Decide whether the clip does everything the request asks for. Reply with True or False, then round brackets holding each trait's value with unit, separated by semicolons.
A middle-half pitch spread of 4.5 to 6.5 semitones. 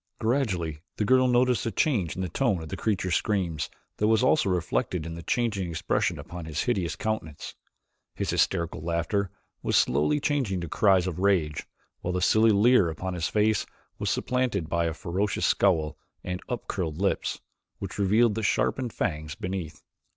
True (4.8 semitones)